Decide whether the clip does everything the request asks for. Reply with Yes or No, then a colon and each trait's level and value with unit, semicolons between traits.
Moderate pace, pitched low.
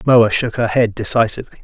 Yes: average, 185 wpm; low, 115 Hz